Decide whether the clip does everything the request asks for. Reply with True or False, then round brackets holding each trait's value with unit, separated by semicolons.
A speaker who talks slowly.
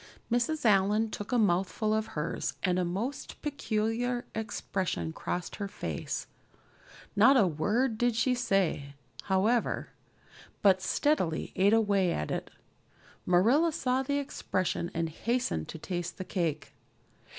True (130 wpm)